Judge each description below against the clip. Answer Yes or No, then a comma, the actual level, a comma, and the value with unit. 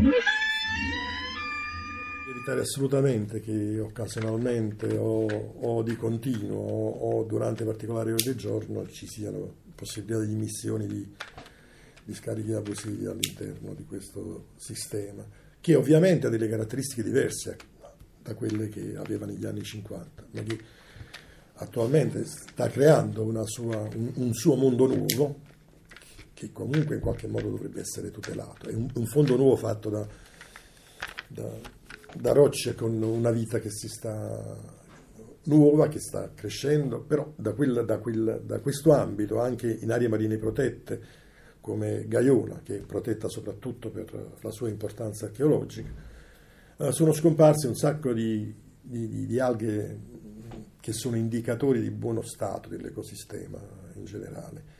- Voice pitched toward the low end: Yes, low, 115 Hz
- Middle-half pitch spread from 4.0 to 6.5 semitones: No, average, 3.6 semitones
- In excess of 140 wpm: No, average, 135 wpm